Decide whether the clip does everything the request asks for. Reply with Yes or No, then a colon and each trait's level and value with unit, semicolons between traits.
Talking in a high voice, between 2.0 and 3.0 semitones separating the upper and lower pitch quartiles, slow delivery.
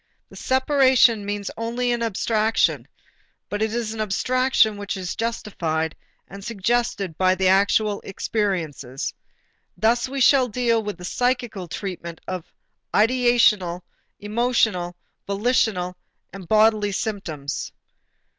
No: high, 210 Hz; average, 4.0 semitones; slow, 115 wpm